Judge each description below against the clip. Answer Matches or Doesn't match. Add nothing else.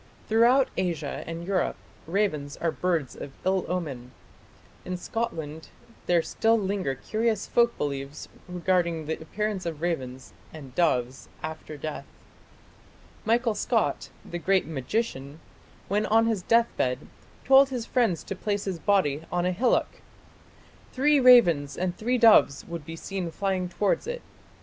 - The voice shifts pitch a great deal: Matches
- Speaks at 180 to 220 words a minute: Doesn't match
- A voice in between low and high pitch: Matches